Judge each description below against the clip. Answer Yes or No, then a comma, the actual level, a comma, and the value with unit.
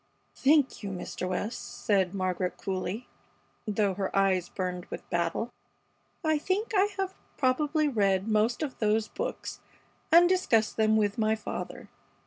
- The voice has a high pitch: Yes, high, 215 Hz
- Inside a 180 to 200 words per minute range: No, average, 140 wpm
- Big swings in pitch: Yes, wide, 7.2 semitones